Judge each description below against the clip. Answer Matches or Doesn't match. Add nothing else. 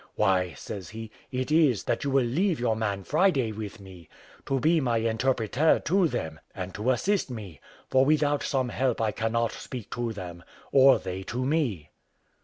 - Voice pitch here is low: Matches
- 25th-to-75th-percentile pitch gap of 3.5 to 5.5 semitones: Matches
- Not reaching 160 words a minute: Doesn't match